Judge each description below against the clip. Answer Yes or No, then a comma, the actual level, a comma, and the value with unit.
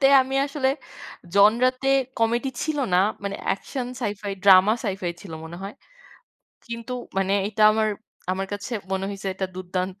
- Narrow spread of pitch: No, average, 3.8 semitones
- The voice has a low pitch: No, high, 205 Hz